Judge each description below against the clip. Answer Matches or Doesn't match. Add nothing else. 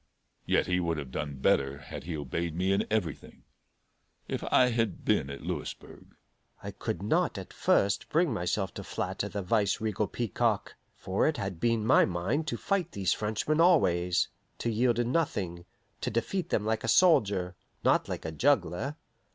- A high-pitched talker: Doesn't match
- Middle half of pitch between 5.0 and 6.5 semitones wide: Matches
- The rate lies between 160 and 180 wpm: Matches